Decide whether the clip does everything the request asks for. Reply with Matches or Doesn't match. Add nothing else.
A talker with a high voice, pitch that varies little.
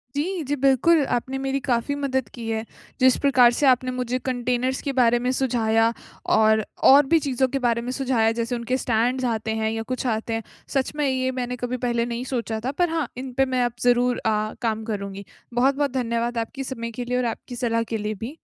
Matches